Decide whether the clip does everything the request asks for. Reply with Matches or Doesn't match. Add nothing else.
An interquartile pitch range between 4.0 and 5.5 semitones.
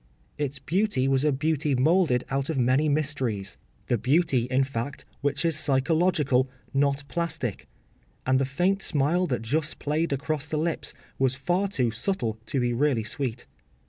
Doesn't match